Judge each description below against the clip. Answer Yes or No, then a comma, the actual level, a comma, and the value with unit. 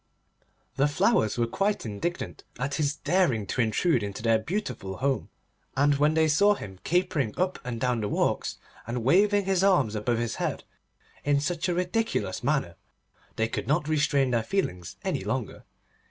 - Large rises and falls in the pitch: Yes, wide, 7.5 semitones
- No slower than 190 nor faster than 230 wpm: No, average, 170 wpm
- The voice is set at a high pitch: No, medium, 140 Hz